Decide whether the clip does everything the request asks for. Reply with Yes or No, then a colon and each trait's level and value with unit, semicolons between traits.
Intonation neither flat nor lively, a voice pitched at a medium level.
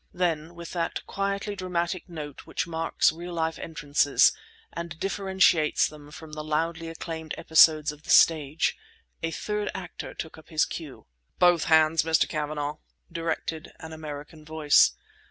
No: narrow, 1.9 semitones; medium, 160 Hz